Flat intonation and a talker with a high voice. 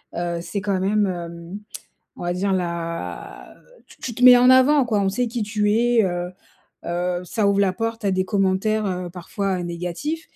No: average, 4.0 semitones; high, 195 Hz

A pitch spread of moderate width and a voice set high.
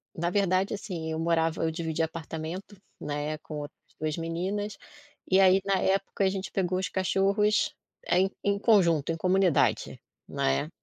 No: average, 3.1 semitones; medium, 180 Hz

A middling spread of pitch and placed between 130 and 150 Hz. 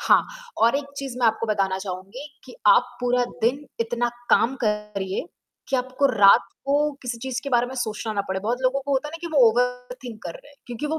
No: average, 3.6 semitones; high, 245 Hz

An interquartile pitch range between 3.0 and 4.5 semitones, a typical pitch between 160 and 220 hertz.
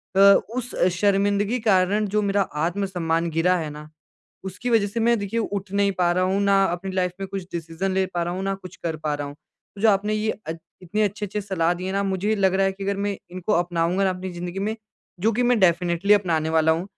No: narrow, 2.6 semitones; high, 190 Hz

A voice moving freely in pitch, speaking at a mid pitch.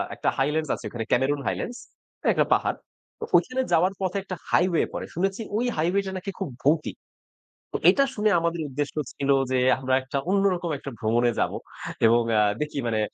Yes: wide, 6.3 semitones; medium, 160 Hz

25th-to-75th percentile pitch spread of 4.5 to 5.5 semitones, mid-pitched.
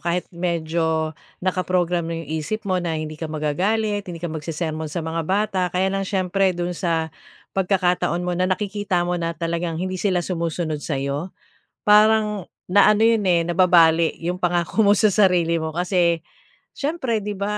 No: average, 2.8 semitones; medium, 175 Hz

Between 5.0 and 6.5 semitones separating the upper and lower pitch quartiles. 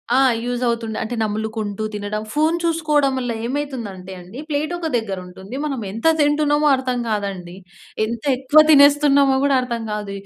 Yes: wide, 5.4 semitones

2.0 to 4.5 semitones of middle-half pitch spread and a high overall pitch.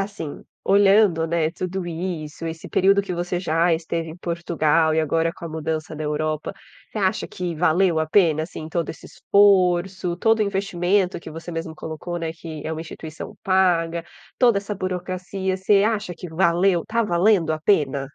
No: average, 3.0 semitones; medium, 175 Hz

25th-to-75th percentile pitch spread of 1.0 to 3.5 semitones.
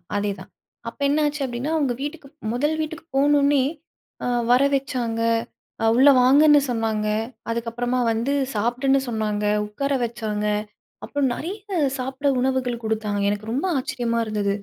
No: average, 4.0 semitones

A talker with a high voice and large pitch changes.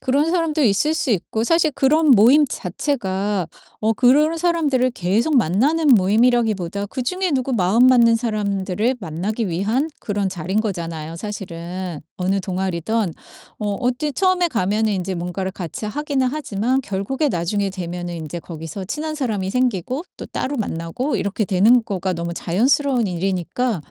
Yes: high, 215 Hz; wide, 5.9 semitones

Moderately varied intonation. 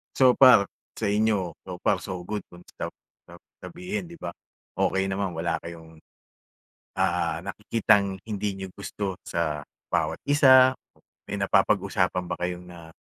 Yes: average, 3.7 semitones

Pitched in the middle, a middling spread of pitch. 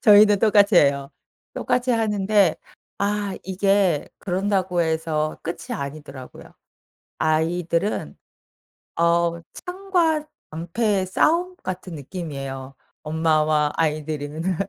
Yes: medium, 175 Hz; average, 4.8 semitones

